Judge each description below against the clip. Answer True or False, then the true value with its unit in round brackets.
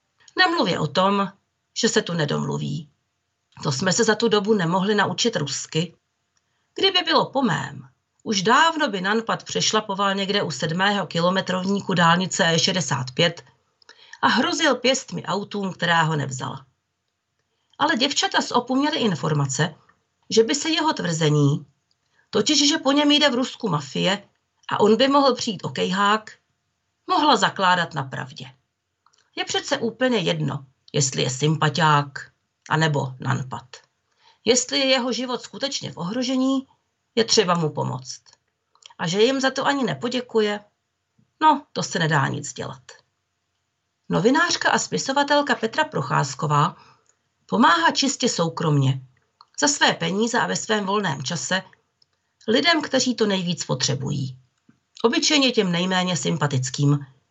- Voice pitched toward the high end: True (195 Hz)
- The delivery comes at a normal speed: True (130 wpm)